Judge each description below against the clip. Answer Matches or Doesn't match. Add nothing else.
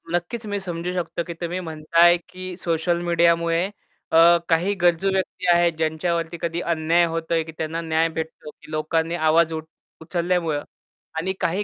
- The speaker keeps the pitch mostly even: Matches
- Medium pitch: Matches